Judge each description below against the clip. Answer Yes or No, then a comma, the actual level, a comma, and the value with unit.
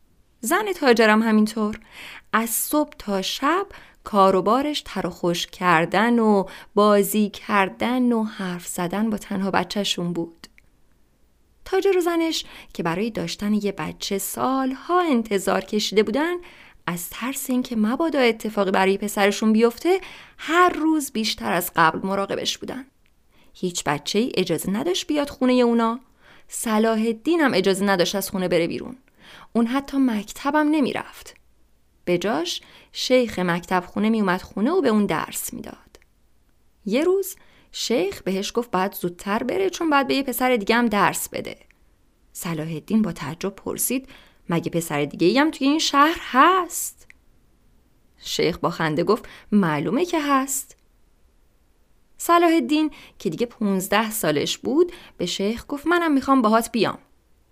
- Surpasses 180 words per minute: No, average, 140 wpm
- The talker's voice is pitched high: Yes, high, 220 Hz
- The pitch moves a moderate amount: No, wide, 6.2 semitones